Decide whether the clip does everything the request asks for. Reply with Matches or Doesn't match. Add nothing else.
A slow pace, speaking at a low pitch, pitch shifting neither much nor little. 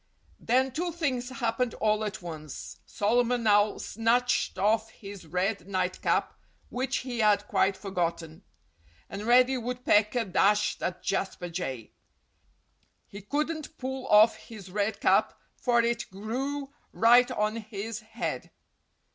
Doesn't match